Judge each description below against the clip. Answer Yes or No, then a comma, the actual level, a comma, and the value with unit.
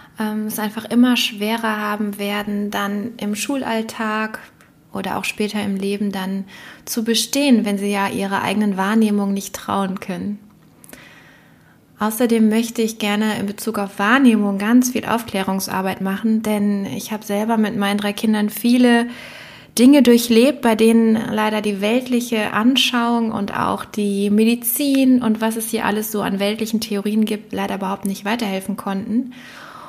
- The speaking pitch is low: No, high, 215 Hz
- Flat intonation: Yes, narrow, 2.1 semitones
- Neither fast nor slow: Yes, average, 150 wpm